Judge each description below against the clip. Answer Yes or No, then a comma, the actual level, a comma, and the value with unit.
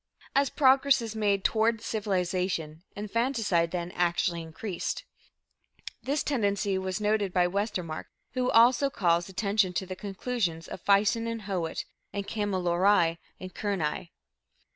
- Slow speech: Yes, slow, 125 wpm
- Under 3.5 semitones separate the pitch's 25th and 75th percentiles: No, average, 4.0 semitones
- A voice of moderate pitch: No, high, 200 Hz